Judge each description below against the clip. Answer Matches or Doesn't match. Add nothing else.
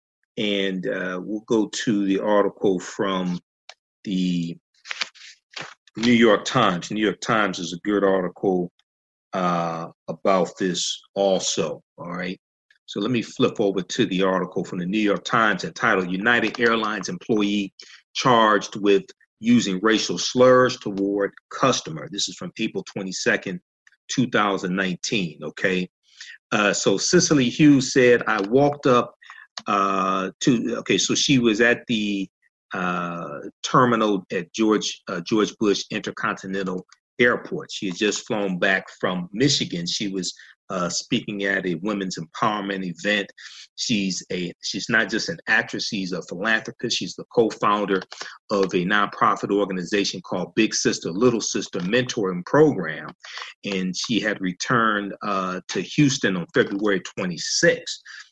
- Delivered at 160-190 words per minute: Doesn't match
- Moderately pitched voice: Doesn't match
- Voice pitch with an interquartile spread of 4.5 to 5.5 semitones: Doesn't match